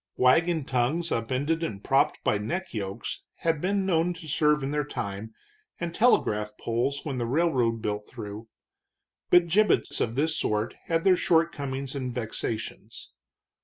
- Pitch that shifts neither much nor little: No, wide, 6.3 semitones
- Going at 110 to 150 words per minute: Yes, average, 145 wpm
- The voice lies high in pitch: No, low, 135 Hz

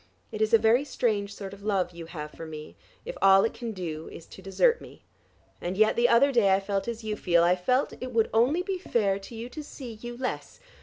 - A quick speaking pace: Yes, fast, 245 wpm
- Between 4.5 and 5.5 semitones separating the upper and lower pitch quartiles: No, average, 3.9 semitones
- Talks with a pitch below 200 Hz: No, high, 215 Hz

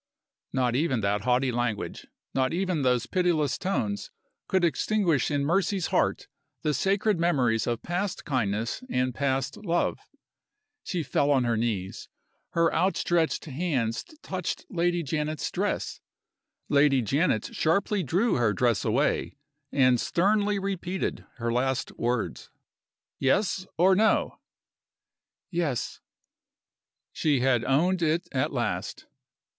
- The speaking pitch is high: No, medium, 145 Hz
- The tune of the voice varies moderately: No, wide, 6.2 semitones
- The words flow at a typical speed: No, slow, 120 wpm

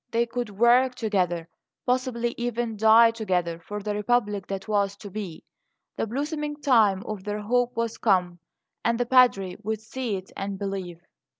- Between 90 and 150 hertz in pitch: No, high, 215 Hz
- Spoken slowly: No, average, 165 wpm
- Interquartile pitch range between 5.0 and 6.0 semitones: No, average, 3.5 semitones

